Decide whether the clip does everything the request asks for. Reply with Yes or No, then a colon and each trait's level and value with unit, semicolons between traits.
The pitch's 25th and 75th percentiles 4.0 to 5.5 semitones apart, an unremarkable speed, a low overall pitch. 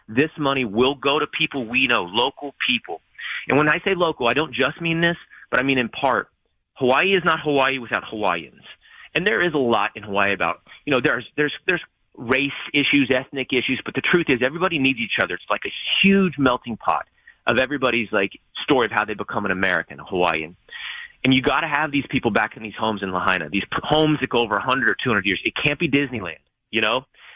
No: average, 4.7 semitones; fast, 225 wpm; low, 130 Hz